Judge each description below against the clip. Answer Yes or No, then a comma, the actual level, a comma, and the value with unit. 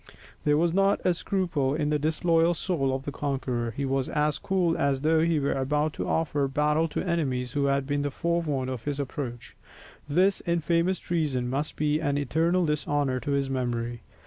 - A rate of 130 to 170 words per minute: No, average, 185 wpm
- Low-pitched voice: No, medium, 145 Hz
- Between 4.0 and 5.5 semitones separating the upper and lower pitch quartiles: No, average, 3.4 semitones